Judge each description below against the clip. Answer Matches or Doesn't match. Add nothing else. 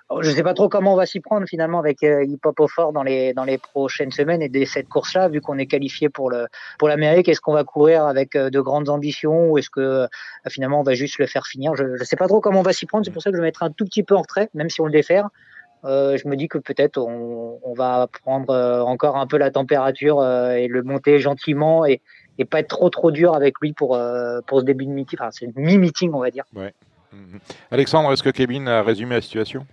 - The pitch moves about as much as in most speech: Matches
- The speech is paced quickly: Matches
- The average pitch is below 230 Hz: Matches